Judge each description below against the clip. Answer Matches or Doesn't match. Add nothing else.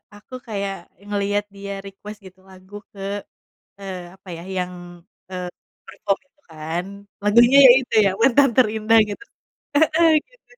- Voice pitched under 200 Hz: Doesn't match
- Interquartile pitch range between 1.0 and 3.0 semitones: Doesn't match